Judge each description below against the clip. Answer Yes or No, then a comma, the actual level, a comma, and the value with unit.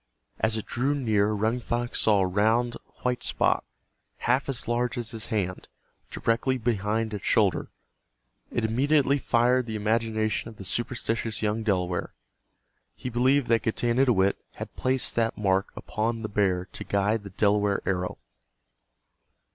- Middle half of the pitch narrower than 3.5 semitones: Yes, average, 2.7 semitones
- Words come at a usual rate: Yes, average, 145 wpm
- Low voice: Yes, low, 110 Hz